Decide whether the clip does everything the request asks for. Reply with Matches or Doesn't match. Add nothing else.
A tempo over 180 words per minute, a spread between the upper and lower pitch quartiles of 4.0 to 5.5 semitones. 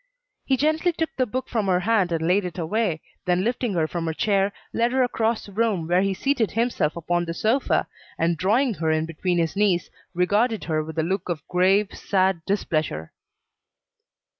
Matches